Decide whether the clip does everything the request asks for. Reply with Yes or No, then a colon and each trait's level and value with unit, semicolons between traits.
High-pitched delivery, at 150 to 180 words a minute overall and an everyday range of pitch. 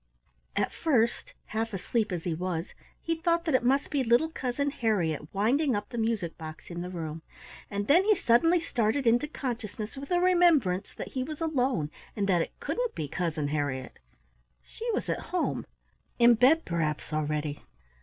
No: high, 230 Hz; average, 175 wpm; wide, 8.7 semitones